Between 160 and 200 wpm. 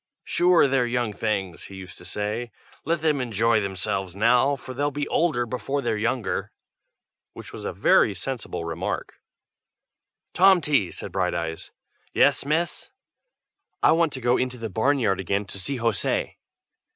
No: average, 150 wpm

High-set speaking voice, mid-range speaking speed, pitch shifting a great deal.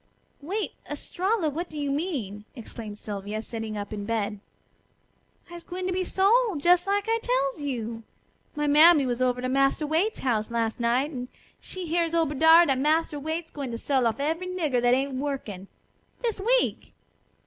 Yes: very high, 285 Hz; average, 175 wpm; wide, 6.4 semitones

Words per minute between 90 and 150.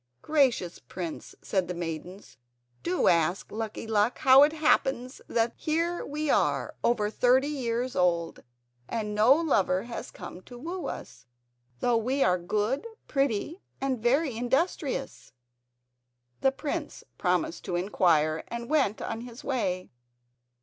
Yes: slow, 135 wpm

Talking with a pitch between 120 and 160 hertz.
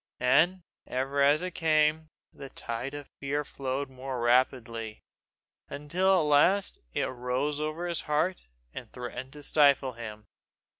Yes: medium, 140 Hz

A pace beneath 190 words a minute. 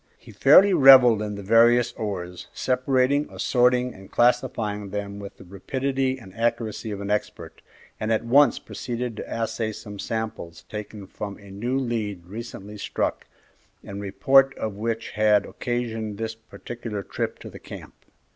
Yes: average, 155 wpm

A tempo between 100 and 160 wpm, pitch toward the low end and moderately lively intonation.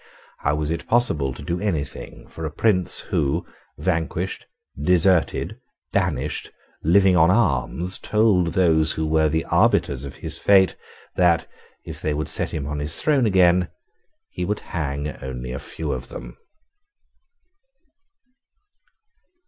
Yes: average, 140 wpm; very low, 80 Hz; average, 3.8 semitones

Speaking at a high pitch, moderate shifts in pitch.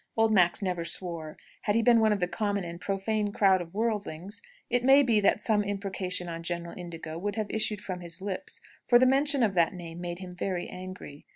Yes: high, 195 Hz; average, 3.6 semitones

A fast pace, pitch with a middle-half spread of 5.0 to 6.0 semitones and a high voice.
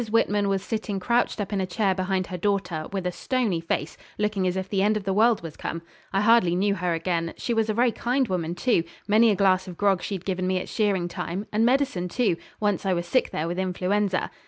No: fast, 240 wpm; average, 2.8 semitones; high, 195 Hz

